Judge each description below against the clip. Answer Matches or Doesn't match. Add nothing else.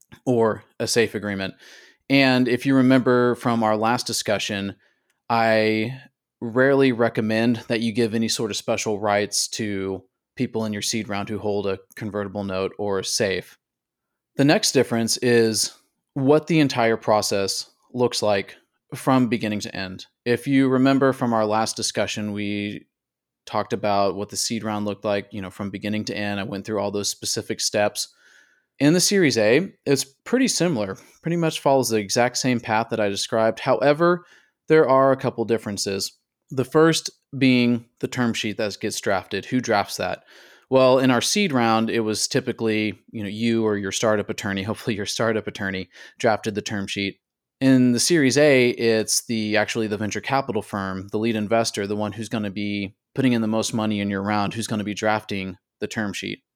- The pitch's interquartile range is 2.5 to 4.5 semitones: Matches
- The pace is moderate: Matches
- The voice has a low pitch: Matches